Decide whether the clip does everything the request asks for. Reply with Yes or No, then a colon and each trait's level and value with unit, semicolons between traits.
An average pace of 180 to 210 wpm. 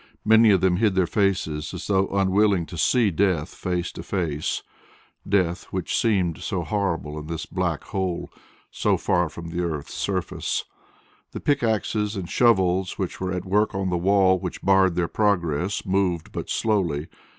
No: average, 165 wpm